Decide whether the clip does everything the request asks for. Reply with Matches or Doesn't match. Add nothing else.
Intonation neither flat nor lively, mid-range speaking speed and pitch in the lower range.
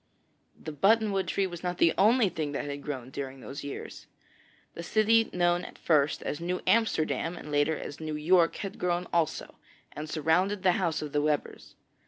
Doesn't match